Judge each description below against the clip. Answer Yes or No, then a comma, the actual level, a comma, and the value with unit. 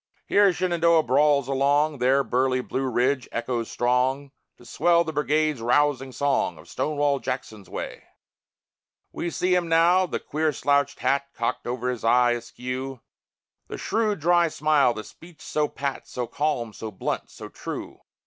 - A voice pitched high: No, medium, 140 Hz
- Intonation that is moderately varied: Yes, average, 3.7 semitones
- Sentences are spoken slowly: No, average, 155 wpm